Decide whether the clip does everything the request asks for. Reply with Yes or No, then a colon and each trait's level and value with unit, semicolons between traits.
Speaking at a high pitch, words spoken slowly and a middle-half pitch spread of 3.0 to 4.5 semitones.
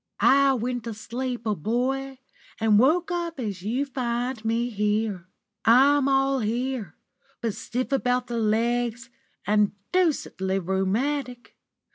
Yes: high, 245 Hz; slow, 115 wpm; average, 3.6 semitones